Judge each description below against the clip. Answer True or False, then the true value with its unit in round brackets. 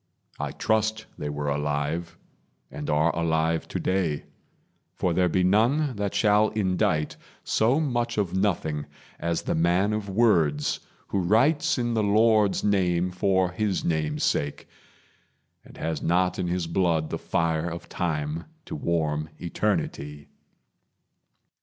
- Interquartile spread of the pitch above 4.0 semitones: True (4.9 semitones)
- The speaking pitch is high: False (90 Hz)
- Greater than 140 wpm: False (135 wpm)